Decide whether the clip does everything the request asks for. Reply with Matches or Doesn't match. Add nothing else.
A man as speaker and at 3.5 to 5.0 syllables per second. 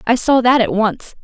Doesn't match